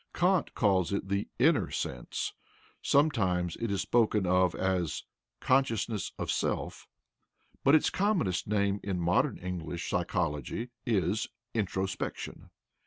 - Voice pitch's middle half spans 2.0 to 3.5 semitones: No, average, 4.2 semitones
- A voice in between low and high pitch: No, low, 100 Hz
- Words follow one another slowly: Yes, slow, 115 wpm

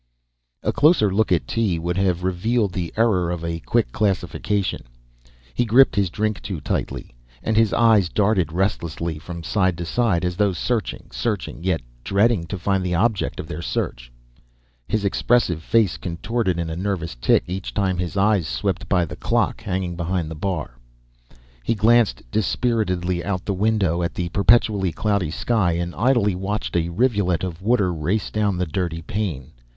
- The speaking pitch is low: Yes, very low, 95 Hz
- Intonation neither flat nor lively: Yes, average, 3.8 semitones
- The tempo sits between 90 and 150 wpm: No, average, 170 wpm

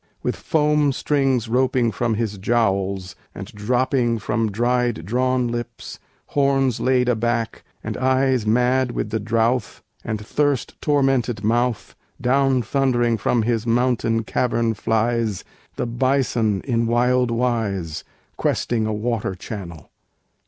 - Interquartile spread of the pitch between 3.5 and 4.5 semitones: No, narrow, 2.6 semitones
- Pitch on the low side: Yes, low, 120 Hz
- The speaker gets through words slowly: Yes, slow, 125 wpm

